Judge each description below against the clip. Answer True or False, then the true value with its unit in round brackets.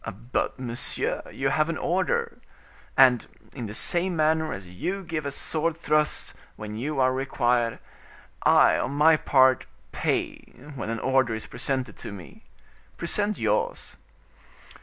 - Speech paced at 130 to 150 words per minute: True (140 wpm)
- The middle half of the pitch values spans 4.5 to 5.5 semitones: True (5.0 semitones)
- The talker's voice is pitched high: False (135 Hz)